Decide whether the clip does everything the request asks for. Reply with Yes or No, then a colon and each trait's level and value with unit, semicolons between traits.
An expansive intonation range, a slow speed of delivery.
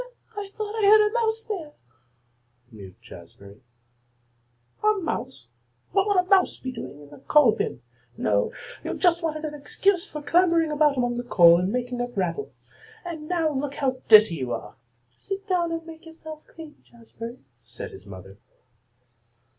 No: wide, 9.0 semitones; average, 170 wpm